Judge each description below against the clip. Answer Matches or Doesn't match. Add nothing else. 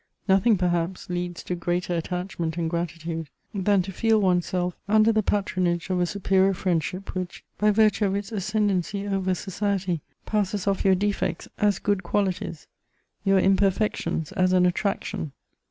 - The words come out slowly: Doesn't match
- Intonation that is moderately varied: Doesn't match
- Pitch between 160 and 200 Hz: Matches